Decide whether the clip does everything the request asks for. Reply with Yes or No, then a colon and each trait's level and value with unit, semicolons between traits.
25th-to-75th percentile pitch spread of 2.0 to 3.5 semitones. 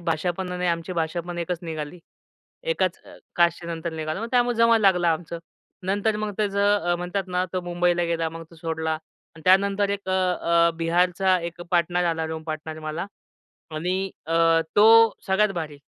Yes: average, 2.8 semitones